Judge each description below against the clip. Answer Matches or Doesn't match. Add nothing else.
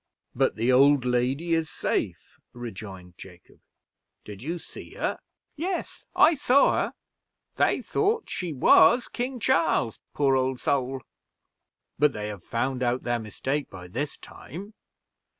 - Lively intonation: Matches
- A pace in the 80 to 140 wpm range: Matches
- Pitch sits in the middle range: Doesn't match